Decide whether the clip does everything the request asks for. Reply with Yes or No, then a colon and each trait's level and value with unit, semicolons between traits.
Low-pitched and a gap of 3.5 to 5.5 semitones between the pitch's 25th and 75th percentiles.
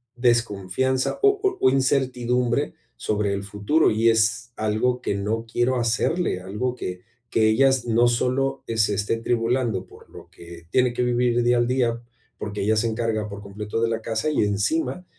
No: low, 115 Hz; average, 2.9 semitones